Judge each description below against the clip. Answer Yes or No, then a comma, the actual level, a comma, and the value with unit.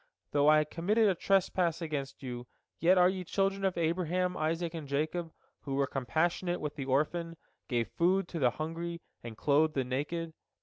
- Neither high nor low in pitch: Yes, medium, 165 Hz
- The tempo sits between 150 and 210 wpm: Yes, average, 175 wpm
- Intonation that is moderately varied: Yes, average, 3.6 semitones